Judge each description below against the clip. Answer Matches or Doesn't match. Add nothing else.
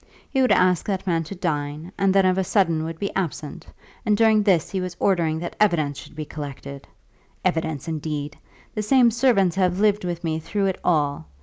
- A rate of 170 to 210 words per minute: Matches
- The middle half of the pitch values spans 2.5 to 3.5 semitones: Doesn't match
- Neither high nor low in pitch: Matches